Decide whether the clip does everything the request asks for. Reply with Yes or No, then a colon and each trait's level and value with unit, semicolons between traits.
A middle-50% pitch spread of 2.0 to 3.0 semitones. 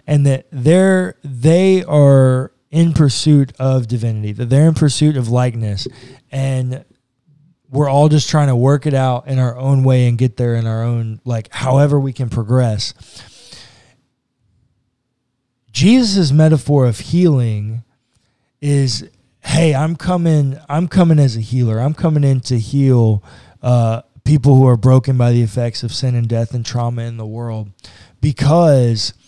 No: average, 3.5 semitones